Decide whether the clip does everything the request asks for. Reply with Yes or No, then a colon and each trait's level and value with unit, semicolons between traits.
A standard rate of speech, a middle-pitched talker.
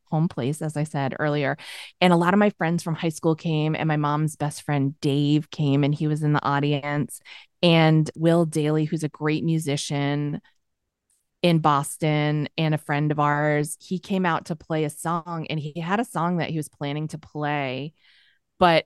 Yes: average, 195 wpm; medium, 155 Hz